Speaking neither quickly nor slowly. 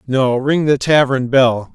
Yes: average, 170 wpm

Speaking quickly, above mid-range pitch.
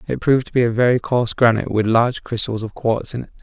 No: fast, 260 wpm; low, 115 Hz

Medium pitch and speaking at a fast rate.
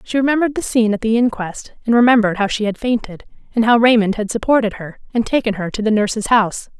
No: high, 225 Hz; fast, 230 wpm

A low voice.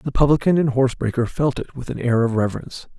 Yes: low, 130 Hz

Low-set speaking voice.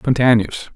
Yes: low, 115 Hz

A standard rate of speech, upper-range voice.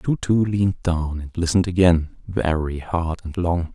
No: average, 175 wpm; very low, 85 Hz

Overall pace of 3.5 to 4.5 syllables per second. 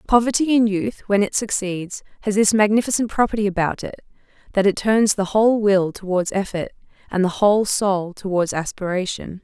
No: 5.2 syllables/s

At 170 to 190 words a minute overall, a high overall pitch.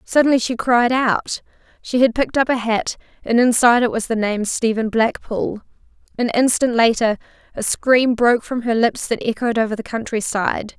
Yes: average, 180 wpm; high, 235 Hz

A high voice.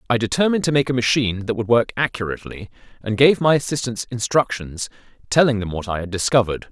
No: low, 120 Hz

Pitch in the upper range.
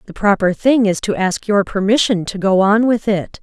Yes: high, 205 Hz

